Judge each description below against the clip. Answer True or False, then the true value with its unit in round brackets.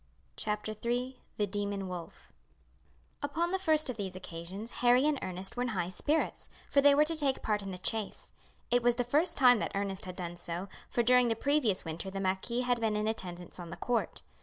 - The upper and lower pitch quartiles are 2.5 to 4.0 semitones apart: False (4.9 semitones)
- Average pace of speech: False (210 wpm)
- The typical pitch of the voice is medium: False (220 Hz)